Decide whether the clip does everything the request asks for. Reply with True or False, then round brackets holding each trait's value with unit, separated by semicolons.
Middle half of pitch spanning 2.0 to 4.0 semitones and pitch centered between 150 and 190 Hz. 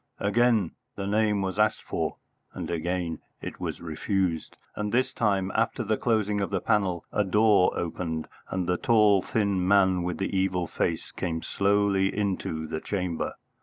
False (2.7 semitones; 95 Hz)